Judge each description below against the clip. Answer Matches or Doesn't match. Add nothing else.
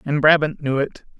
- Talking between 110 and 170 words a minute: Doesn't match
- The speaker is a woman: Doesn't match